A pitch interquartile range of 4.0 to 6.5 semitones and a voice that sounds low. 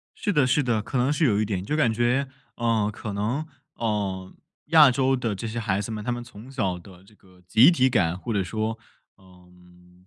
Yes: average, 4.7 semitones; low, 110 Hz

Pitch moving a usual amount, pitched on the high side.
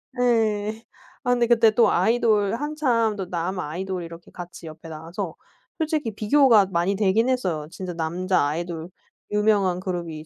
Yes: average, 4.8 semitones; high, 195 Hz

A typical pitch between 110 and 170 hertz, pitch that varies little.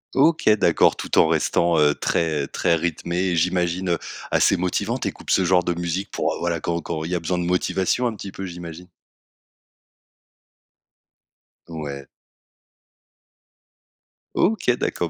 No: very low, 85 Hz; narrow, 2.1 semitones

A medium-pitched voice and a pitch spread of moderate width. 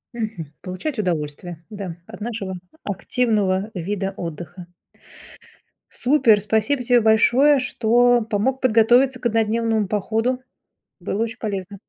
No: high, 220 Hz; average, 3.8 semitones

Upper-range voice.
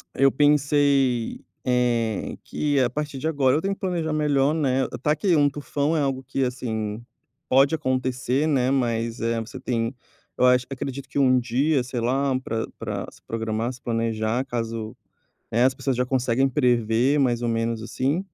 No: low, 130 Hz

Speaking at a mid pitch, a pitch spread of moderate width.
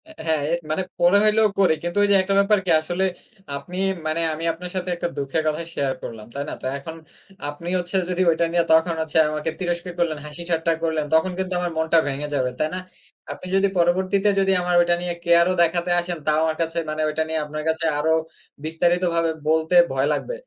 No: medium, 170 Hz; narrow, 2.2 semitones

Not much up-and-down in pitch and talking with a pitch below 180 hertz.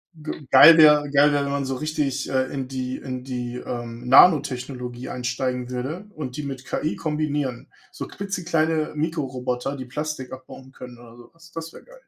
No: average, 3.3 semitones; low, 135 Hz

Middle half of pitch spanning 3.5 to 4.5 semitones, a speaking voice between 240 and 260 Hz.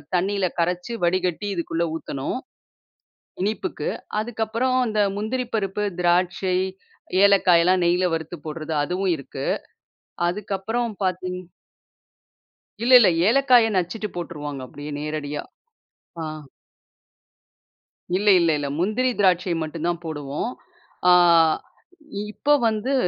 No: average, 4.1 semitones; medium, 185 Hz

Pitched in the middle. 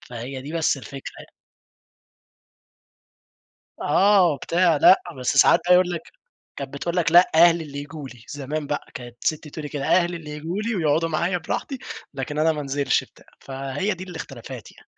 Yes: medium, 155 Hz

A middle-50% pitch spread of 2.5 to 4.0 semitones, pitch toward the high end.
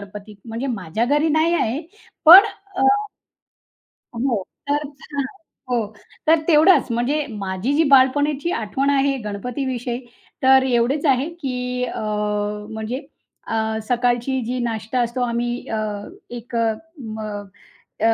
Yes: average, 3.7 semitones; very high, 250 Hz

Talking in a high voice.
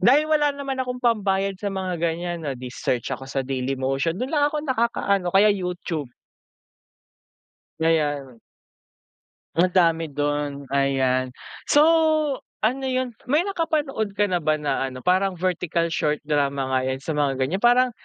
No: medium, 175 Hz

